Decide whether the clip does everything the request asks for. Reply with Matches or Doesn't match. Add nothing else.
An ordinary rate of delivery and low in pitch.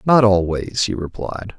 Matches